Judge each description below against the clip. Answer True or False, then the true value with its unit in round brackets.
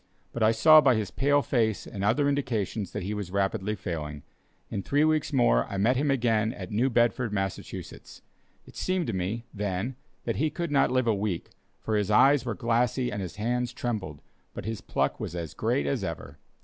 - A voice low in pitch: True (110 Hz)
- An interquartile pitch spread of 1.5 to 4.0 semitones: False (4.6 semitones)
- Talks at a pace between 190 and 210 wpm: True (200 wpm)